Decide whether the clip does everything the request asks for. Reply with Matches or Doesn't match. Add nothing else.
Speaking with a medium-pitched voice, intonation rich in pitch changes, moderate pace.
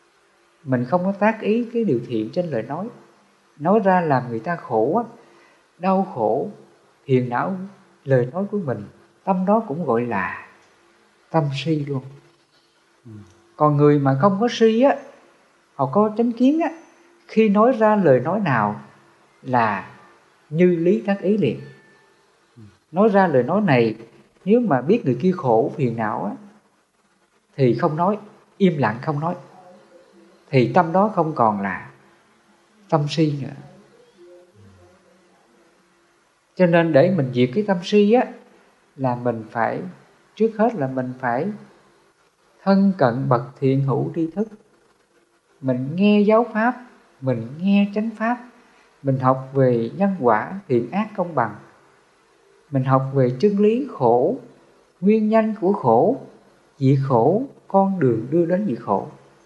Matches